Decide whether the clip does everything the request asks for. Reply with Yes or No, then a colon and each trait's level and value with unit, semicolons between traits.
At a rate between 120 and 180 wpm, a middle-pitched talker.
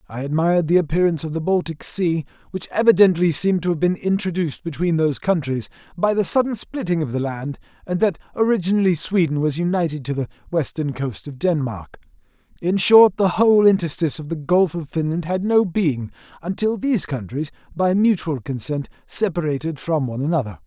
Yes: average, 175 wpm; medium, 165 Hz